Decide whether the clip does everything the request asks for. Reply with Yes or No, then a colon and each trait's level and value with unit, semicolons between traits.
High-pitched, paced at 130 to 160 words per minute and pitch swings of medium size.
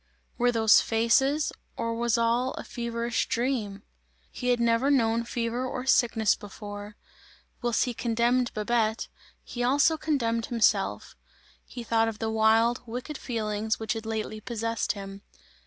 No: high, 230 Hz; average, 140 wpm; narrow, 1.7 semitones